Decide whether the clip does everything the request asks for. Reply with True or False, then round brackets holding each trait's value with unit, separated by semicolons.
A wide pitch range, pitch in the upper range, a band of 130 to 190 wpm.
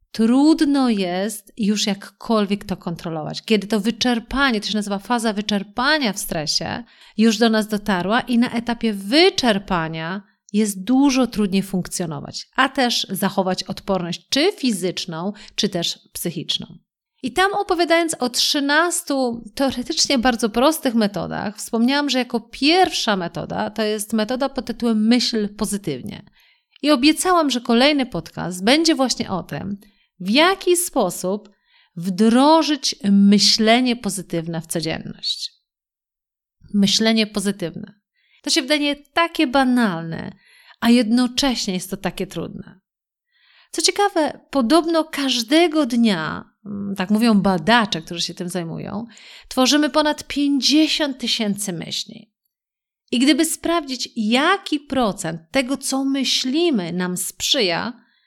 False (5.9 semitones; 230 Hz; 120 wpm)